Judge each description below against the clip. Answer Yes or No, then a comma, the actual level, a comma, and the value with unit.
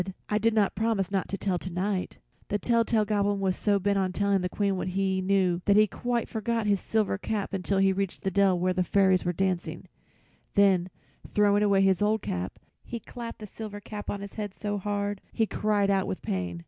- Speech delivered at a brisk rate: Yes, fast, 225 wpm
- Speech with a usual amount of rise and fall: No, narrow, 1.8 semitones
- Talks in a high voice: Yes, high, 200 Hz